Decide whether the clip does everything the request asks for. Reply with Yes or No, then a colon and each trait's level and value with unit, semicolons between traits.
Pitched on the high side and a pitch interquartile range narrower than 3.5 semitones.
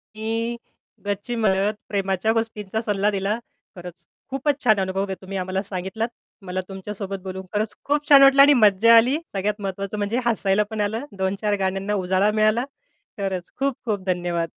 Yes: high, 205 Hz; average, 2.9 semitones